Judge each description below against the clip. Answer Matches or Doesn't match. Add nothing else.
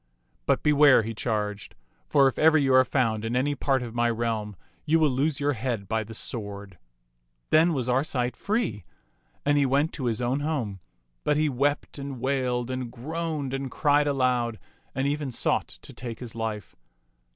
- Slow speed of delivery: Doesn't match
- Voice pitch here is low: Matches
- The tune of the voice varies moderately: Matches